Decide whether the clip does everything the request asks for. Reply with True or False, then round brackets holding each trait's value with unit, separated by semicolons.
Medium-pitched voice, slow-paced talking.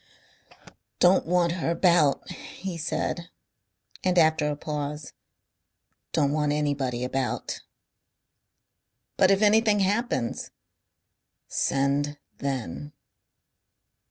True (150 Hz; 90 wpm)